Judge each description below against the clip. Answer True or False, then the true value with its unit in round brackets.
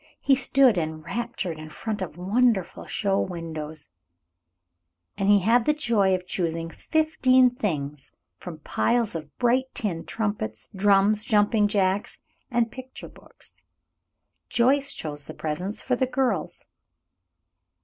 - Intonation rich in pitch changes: True (6.5 semitones)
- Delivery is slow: True (125 wpm)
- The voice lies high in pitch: True (205 Hz)